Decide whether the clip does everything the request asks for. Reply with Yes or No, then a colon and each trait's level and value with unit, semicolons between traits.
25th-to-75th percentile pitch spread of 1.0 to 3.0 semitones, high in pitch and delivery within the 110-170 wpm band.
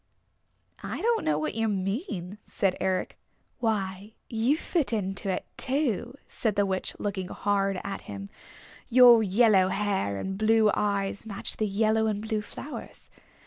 Yes: average, 2.7 semitones; high, 205 Hz; average, 145 wpm